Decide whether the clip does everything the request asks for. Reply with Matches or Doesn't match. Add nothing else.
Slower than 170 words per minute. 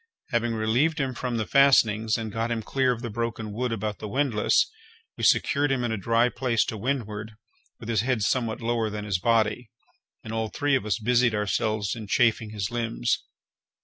Doesn't match